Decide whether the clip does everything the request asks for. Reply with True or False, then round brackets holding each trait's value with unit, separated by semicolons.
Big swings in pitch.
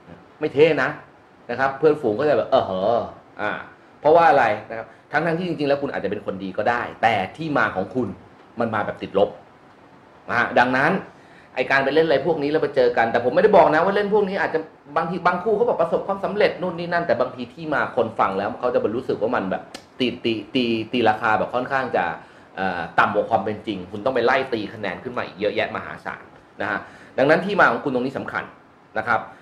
True (7.4 semitones)